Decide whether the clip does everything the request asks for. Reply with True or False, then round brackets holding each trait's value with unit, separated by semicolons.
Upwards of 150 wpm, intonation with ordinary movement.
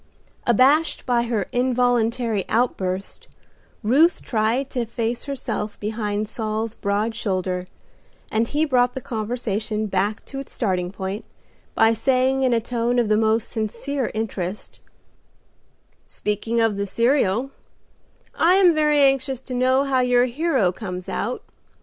False (135 wpm; 3.4 semitones)